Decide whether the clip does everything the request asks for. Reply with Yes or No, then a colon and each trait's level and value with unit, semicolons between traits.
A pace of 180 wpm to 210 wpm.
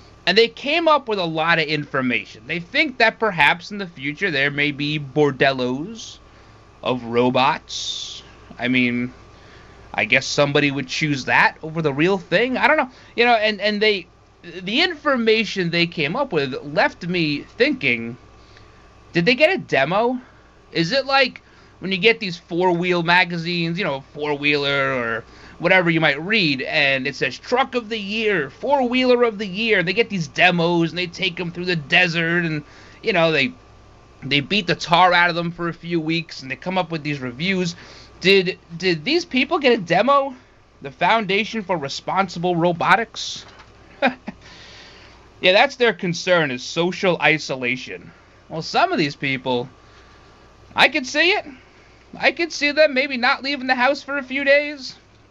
No: average, 170 wpm